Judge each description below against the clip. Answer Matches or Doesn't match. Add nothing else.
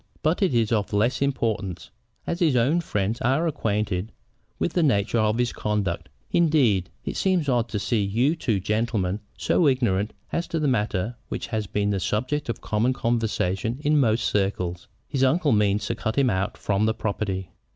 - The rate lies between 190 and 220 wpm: Doesn't match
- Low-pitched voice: Matches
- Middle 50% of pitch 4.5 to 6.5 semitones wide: Matches